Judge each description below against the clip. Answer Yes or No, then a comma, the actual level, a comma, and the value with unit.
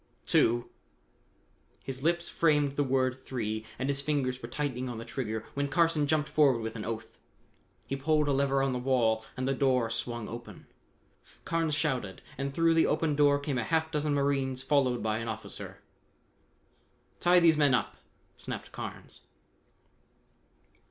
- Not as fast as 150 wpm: No, average, 160 wpm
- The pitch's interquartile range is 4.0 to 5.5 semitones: No, average, 3.4 semitones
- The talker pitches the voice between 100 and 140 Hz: Yes, low, 135 Hz